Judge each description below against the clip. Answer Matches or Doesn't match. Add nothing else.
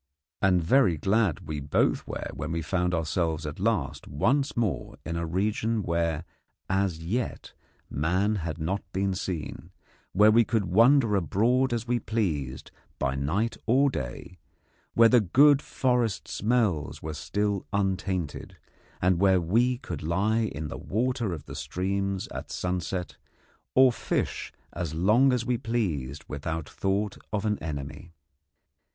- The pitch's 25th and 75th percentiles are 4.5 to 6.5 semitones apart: Matches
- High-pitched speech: Doesn't match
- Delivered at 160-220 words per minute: Doesn't match